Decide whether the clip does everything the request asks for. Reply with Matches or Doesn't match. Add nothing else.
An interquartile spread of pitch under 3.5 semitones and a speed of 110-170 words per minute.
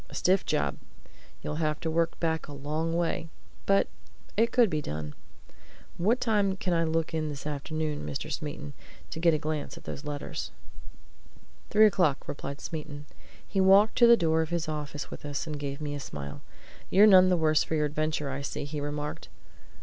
Doesn't match